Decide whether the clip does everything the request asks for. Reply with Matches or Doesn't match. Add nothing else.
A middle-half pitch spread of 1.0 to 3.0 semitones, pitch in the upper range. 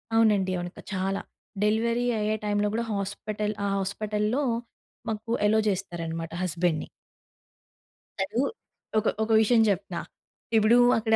Matches